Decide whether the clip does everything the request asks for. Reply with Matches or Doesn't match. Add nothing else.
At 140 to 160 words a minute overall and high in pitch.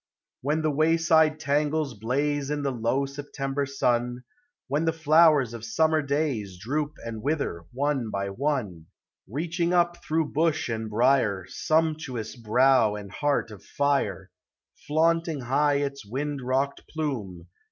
Doesn't match